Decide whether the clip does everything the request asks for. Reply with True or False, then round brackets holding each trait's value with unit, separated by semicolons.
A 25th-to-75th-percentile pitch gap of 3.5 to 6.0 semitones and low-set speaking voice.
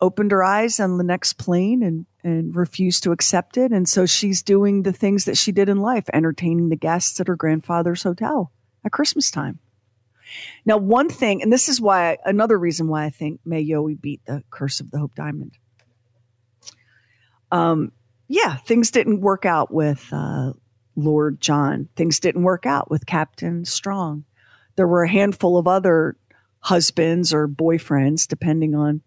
False (4.8 semitones; 165 Hz)